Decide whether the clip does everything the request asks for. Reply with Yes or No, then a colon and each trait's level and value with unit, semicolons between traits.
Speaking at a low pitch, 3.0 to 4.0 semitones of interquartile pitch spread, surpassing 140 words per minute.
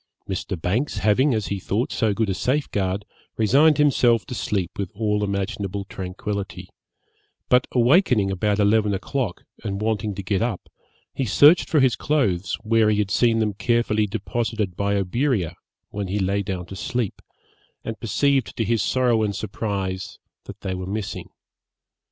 Yes: low, 105 Hz; average, 3.3 semitones; average, 160 wpm